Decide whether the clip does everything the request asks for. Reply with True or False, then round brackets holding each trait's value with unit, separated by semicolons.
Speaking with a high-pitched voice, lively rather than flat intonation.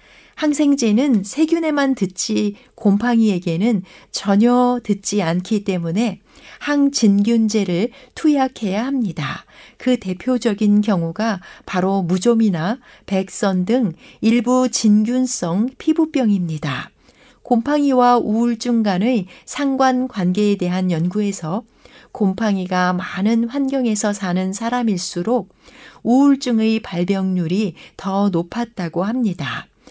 False (215 Hz; 4.5 semitones)